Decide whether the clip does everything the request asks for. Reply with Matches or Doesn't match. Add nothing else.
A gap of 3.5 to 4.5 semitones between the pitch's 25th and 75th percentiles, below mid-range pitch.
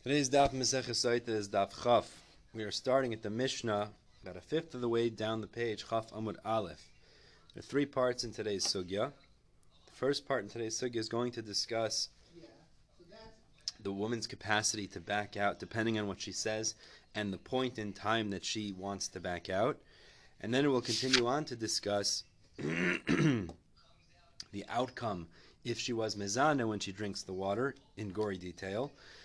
Doesn't match